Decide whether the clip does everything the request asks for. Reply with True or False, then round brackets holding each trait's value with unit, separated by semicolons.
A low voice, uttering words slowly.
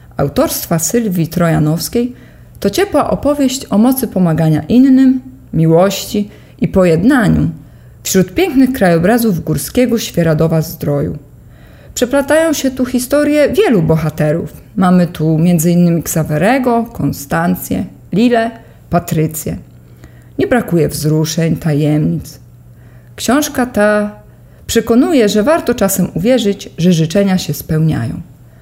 False (185 Hz; 100 wpm)